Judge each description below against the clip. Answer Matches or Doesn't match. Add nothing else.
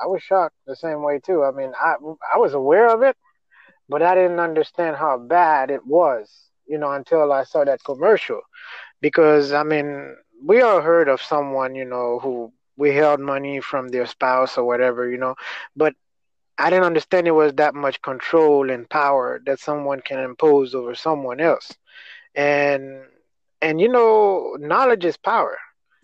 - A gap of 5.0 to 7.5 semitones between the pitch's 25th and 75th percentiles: Doesn't match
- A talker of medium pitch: Matches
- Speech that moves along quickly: Doesn't match